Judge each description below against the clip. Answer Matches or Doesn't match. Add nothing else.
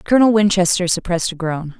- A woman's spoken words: Matches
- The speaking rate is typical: Matches